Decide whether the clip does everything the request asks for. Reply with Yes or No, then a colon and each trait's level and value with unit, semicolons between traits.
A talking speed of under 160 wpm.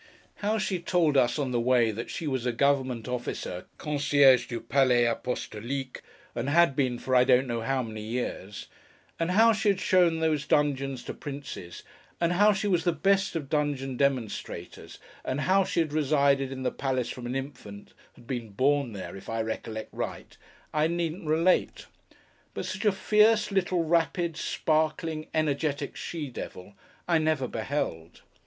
No: average, 165 wpm